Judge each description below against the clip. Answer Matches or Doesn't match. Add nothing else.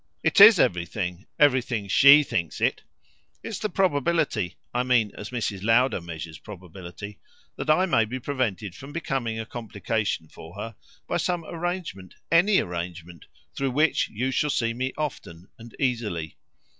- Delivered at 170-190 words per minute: Doesn't match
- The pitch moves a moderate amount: Doesn't match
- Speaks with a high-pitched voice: Doesn't match